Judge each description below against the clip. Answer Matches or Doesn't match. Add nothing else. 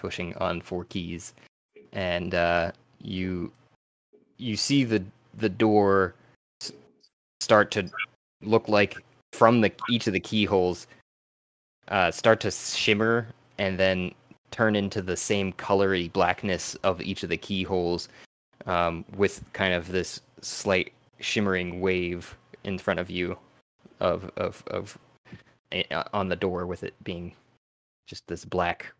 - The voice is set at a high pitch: Doesn't match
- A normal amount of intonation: Matches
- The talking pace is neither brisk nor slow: Doesn't match